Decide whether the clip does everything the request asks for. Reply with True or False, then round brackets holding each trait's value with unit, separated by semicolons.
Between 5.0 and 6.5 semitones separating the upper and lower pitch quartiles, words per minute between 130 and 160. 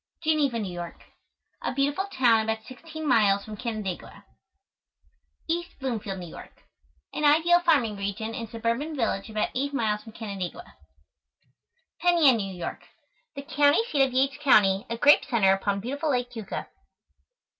True (5.4 semitones; 150 wpm)